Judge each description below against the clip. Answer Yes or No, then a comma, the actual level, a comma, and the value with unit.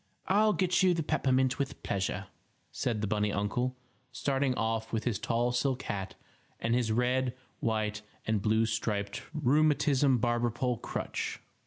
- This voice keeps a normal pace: Yes, average, 150 wpm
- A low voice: Yes, low, 120 Hz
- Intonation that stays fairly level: No, average, 3.5 semitones